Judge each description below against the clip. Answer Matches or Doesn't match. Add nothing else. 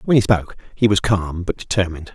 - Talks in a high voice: Doesn't match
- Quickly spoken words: Matches